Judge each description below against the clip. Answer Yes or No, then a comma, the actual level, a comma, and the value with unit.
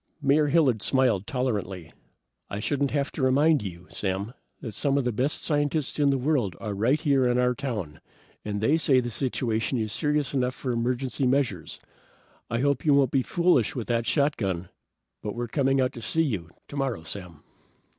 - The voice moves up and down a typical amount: Yes, average, 4.6 semitones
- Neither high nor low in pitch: No, low, 125 Hz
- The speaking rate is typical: Yes, average, 185 wpm